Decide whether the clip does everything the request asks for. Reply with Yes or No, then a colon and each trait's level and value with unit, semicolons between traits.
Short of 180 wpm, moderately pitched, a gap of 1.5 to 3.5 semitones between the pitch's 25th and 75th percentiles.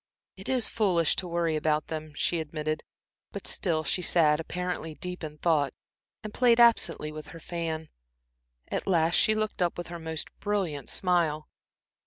Yes: average, 165 wpm; medium, 165 Hz; average, 2.7 semitones